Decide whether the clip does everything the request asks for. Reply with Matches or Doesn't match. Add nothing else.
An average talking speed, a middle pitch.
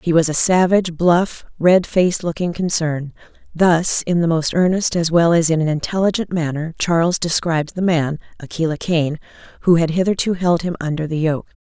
Matches